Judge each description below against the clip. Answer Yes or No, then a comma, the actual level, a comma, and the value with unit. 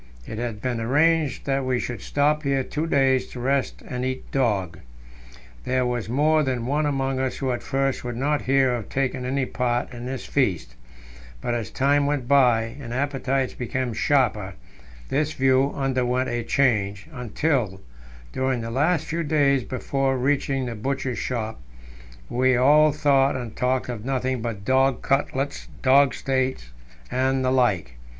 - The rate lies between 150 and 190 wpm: Yes, average, 160 wpm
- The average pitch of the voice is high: No, low, 130 Hz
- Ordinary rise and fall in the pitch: No, narrow, 2.2 semitones